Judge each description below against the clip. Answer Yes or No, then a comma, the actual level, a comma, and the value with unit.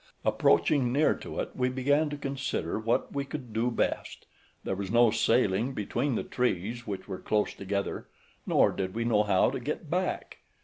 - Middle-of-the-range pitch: No, low, 120 Hz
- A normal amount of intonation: Yes, average, 4.5 semitones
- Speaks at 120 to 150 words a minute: No, average, 180 wpm